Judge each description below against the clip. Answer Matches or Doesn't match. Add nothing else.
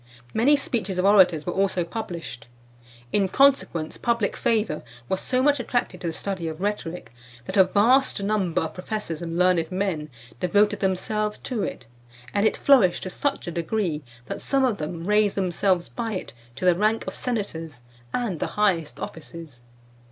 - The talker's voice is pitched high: Matches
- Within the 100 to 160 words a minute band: Doesn't match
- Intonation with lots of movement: Doesn't match